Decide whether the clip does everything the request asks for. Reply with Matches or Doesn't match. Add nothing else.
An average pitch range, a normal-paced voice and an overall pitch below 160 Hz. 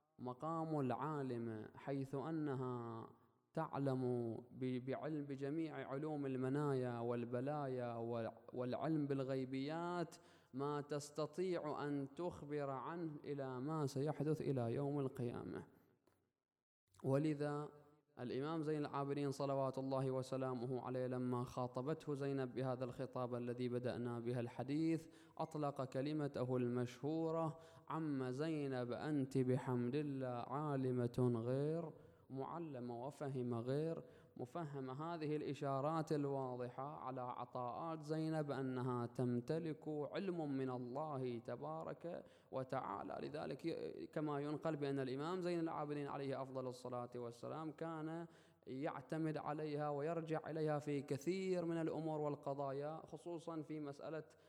Matches